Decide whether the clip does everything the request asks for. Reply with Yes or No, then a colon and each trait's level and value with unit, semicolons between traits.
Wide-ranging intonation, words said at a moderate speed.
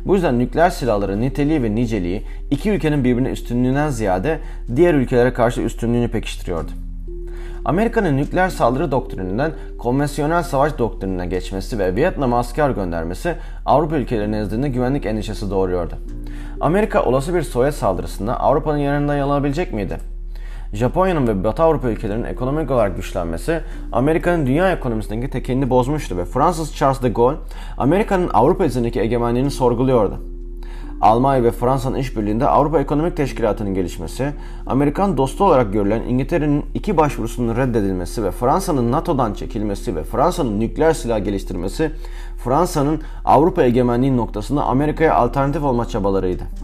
Yes: wide, 5.8 semitones; average, 130 wpm